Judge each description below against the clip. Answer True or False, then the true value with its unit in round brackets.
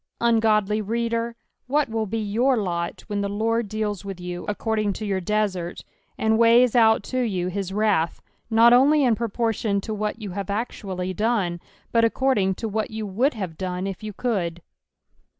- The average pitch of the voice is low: False (215 Hz)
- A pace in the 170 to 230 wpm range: True (175 wpm)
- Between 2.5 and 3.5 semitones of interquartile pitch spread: True (2.9 semitones)